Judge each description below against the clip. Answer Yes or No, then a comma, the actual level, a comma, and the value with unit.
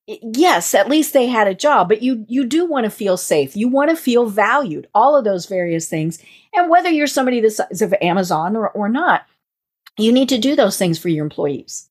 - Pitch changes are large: Yes, wide, 6.4 semitones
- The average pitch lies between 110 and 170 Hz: No, high, 230 Hz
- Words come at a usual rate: No, fast, 220 wpm